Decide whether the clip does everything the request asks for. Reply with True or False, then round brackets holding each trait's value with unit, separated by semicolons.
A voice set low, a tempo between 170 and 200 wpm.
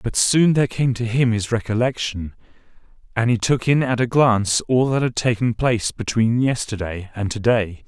True (115 Hz; 190 wpm)